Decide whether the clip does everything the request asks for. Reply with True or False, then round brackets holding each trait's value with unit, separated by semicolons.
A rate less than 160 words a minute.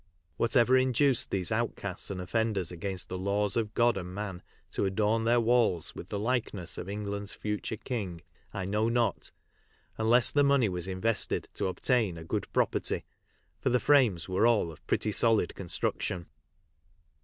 False (165 wpm)